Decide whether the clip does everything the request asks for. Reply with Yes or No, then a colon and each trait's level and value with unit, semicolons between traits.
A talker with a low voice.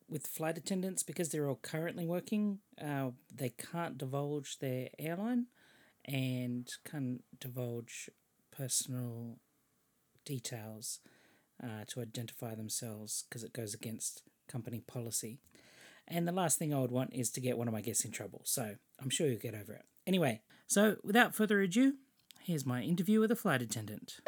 Yes: low, 130 Hz